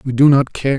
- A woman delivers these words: No, male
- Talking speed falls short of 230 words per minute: No, fast, 305 wpm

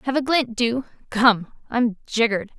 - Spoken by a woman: Yes, female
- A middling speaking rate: Yes, average, 160 wpm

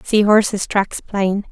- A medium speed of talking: Yes, average, 160 wpm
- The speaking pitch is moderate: No, high, 205 Hz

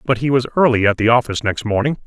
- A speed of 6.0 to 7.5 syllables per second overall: Yes, 7.1 syllables/s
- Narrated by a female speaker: No, male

